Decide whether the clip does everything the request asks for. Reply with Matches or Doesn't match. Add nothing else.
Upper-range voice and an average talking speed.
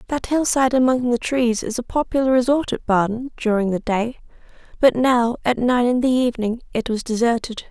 Matches